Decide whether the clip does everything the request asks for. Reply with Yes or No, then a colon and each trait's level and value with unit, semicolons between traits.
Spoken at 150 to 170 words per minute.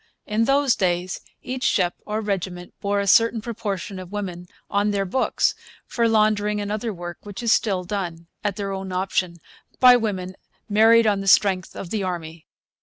No: average, 180 wpm